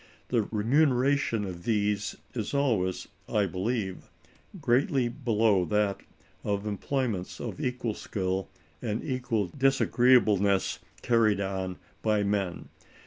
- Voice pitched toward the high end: No, low, 105 Hz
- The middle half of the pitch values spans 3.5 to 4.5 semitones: Yes, average, 4.0 semitones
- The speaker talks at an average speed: No, slow, 105 wpm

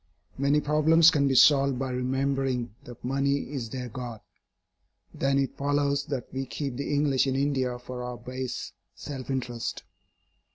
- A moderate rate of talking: Yes, average, 155 wpm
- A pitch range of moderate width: No, narrow, 2.0 semitones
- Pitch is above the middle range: No, low, 135 Hz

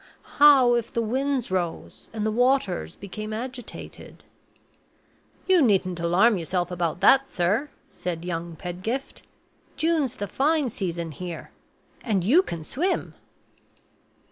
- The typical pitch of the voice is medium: No, high, 215 Hz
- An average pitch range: No, wide, 6.8 semitones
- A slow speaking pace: Yes, slow, 120 wpm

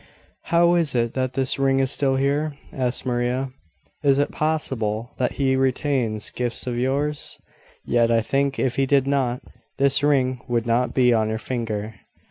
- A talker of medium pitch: No, low, 130 Hz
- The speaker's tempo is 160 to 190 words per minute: Yes, average, 170 wpm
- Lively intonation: No, narrow, 2.5 semitones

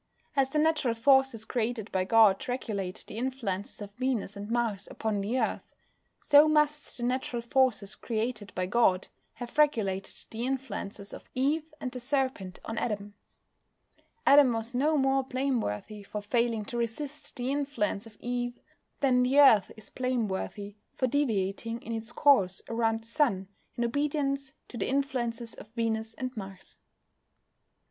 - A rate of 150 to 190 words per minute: Yes, average, 155 wpm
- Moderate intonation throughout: Yes, average, 4.0 semitones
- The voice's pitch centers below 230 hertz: No, high, 235 Hz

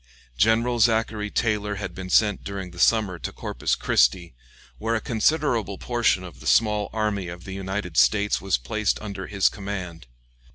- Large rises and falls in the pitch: No, average, 3.0 semitones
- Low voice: Yes, low, 100 Hz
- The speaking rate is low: No, average, 165 wpm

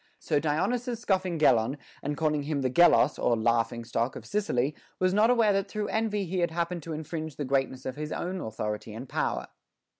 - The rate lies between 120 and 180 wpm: No, average, 200 wpm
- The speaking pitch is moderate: Yes, medium, 155 Hz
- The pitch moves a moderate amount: No, wide, 6.3 semitones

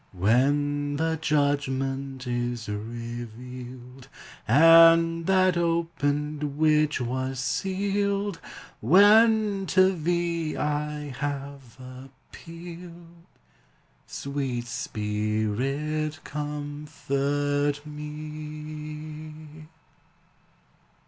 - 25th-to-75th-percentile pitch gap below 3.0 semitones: No, average, 3.8 semitones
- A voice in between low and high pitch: Yes, medium, 150 Hz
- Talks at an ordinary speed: No, slow, 60 wpm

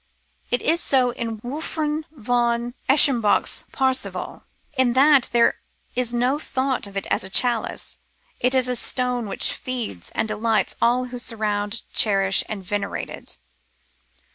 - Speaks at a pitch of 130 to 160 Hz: No, high, 245 Hz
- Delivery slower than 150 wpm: Yes, average, 140 wpm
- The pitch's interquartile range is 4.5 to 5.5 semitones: No, average, 3.0 semitones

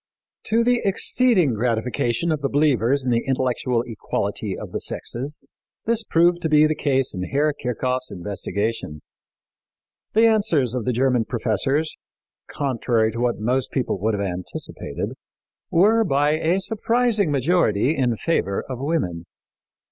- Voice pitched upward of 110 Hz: Yes, low, 135 Hz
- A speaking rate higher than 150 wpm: No, average, 140 wpm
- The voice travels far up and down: Yes, wide, 5.9 semitones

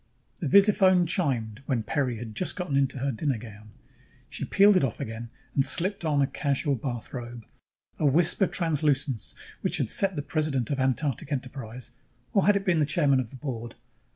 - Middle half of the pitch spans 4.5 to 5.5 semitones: Yes, average, 5.2 semitones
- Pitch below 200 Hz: Yes, medium, 140 Hz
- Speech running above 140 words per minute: Yes, average, 185 wpm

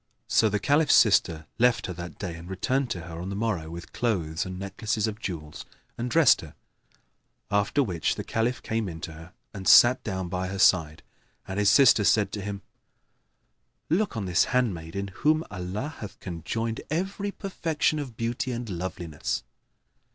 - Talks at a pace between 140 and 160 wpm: No, average, 175 wpm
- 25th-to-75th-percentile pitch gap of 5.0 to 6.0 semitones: Yes, average, 5.3 semitones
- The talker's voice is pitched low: Yes, low, 100 Hz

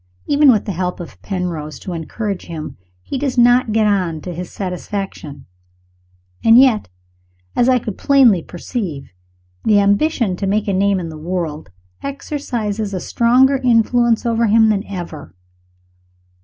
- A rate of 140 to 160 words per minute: Yes, average, 150 wpm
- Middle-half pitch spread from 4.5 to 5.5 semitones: Yes, average, 5.0 semitones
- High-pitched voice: Yes, high, 205 Hz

